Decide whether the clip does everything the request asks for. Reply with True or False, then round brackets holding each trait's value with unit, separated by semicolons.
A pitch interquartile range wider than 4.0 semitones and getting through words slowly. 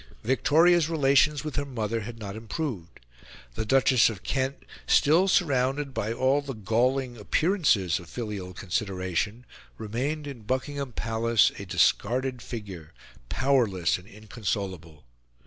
True (5.1 semitones; 125 wpm)